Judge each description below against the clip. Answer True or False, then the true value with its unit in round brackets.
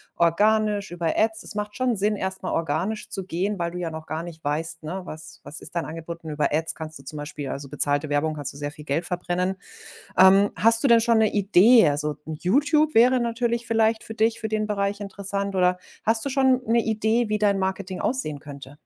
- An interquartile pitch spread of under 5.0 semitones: False (5.6 semitones)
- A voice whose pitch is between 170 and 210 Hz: True (190 Hz)